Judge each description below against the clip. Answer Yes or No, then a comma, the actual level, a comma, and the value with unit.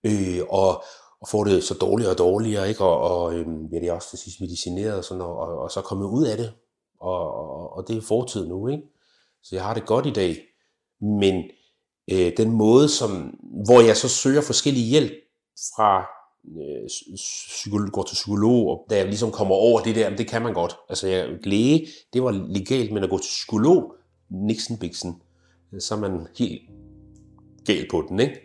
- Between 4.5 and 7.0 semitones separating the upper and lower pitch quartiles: No, average, 3.5 semitones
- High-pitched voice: No, low, 105 Hz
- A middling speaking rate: Yes, average, 200 wpm